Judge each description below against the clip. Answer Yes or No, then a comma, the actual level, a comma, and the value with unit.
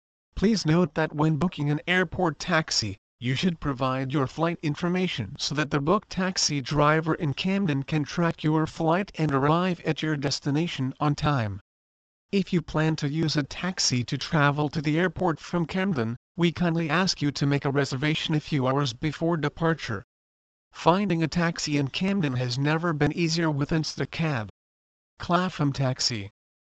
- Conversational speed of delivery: Yes, average, 165 wpm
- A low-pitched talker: No, medium, 155 Hz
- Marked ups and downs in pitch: No, average, 3.7 semitones